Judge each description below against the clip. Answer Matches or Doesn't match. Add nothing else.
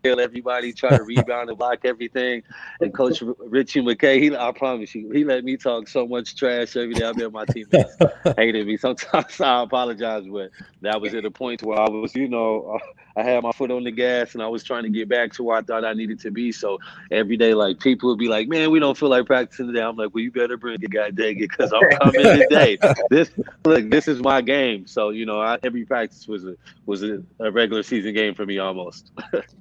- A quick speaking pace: Matches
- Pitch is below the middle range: Matches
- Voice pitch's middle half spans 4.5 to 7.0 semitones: Doesn't match